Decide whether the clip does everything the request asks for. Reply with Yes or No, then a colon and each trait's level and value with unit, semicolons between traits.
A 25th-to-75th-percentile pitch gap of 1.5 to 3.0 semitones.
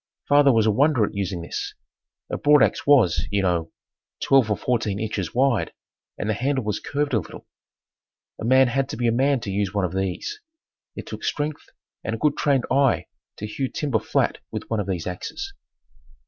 No: wide, 5.4 semitones